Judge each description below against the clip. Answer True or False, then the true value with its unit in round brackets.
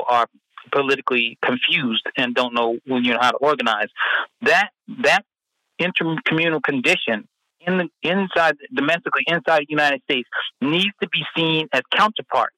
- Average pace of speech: True (145 wpm)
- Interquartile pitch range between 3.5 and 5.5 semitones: True (4.9 semitones)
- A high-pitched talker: False (150 Hz)